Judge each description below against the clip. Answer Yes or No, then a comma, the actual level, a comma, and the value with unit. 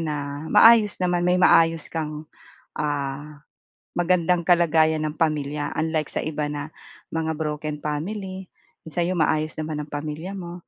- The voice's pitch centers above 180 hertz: No, medium, 155 Hz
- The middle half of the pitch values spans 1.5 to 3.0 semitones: Yes, narrow, 2.6 semitones